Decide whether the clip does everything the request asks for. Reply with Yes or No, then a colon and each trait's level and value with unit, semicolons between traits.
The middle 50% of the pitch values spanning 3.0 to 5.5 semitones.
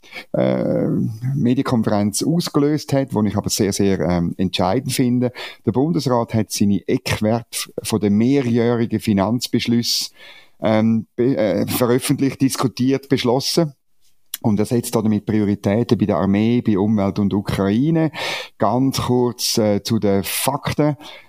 Yes: average, 4.1 semitones